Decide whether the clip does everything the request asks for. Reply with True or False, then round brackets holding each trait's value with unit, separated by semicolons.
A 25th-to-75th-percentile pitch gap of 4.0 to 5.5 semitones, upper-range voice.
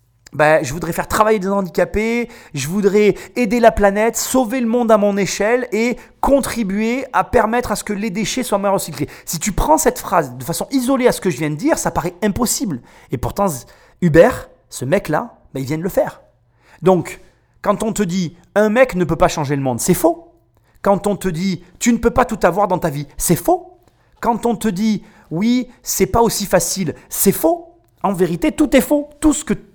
True (5.1 semitones; 205 Hz)